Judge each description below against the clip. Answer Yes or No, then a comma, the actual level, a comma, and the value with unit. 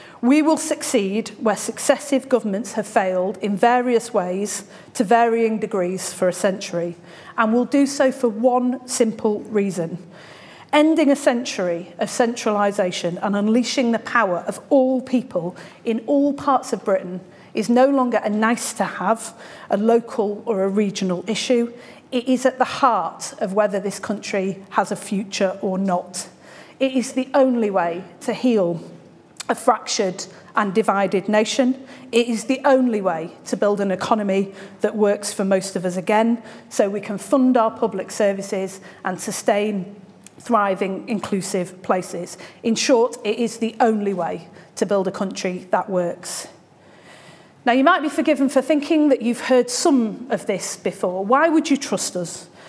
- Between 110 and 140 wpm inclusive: No, average, 160 wpm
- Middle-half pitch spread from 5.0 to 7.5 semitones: No, average, 4.2 semitones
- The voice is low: No, high, 215 Hz